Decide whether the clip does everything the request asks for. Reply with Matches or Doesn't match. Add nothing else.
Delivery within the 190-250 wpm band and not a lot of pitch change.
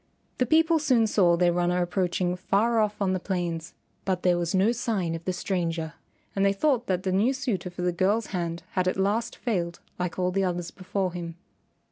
Doesn't match